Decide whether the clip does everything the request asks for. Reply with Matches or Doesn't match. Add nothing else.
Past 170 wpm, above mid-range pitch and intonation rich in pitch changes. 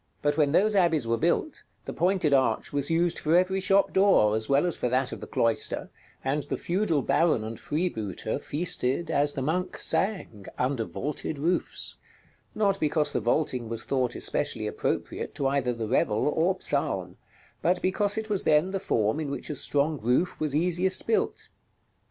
Doesn't match